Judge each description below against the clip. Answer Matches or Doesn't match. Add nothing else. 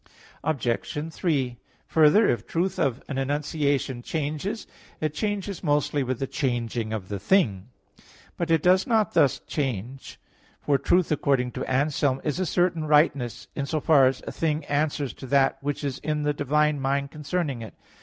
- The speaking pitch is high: Doesn't match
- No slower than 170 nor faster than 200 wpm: Matches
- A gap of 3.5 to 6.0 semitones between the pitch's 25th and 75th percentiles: Doesn't match